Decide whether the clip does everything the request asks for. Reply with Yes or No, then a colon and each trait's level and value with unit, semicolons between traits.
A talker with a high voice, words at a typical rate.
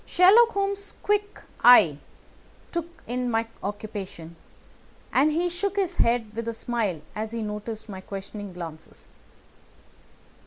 No: high, 230 Hz; slow, 125 wpm